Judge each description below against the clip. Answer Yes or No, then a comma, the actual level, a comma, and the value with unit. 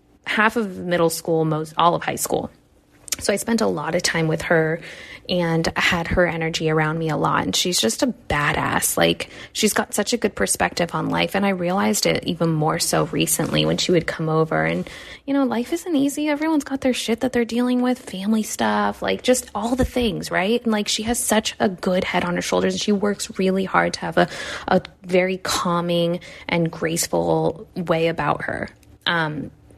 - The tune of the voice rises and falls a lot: Yes, wide, 5.8 semitones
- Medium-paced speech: No, fast, 210 wpm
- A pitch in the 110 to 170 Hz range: No, medium, 185 Hz